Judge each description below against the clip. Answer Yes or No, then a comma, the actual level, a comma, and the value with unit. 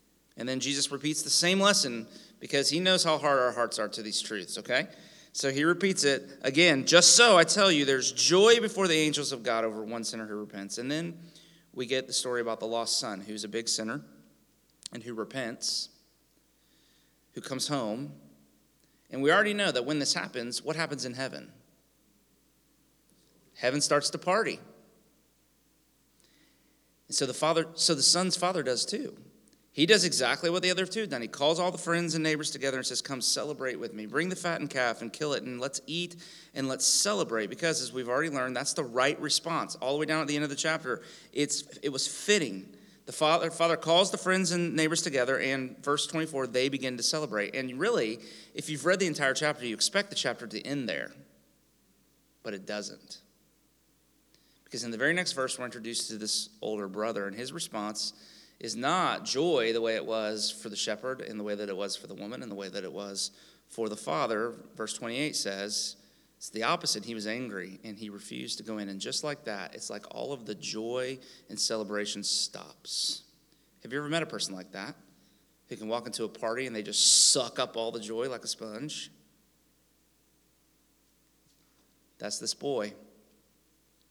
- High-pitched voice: No, low, 130 Hz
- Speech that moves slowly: No, average, 200 wpm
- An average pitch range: No, wide, 6.4 semitones